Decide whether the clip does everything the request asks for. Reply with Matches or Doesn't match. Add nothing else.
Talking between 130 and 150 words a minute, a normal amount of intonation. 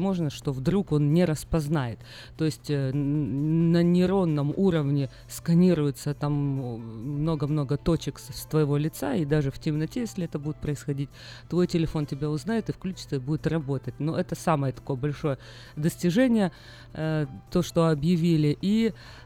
Matches